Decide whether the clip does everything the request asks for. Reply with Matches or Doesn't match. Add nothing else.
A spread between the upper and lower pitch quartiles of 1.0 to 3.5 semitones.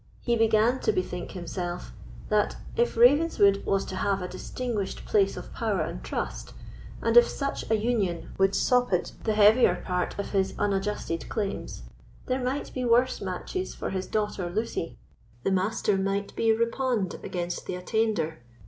Doesn't match